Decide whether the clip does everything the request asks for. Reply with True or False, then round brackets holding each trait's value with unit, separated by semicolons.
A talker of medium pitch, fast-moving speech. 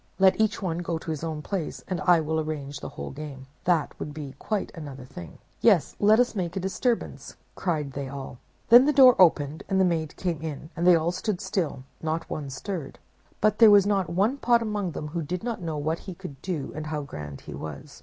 True (165 Hz; 225 wpm)